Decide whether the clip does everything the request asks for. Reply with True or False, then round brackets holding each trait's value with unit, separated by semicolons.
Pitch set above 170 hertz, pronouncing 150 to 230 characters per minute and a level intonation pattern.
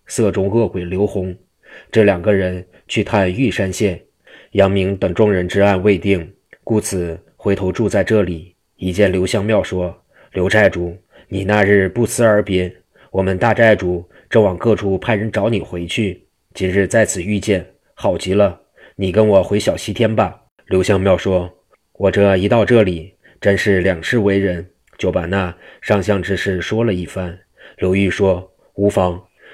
False (95 Hz; 225 characters per minute; 2.3 semitones)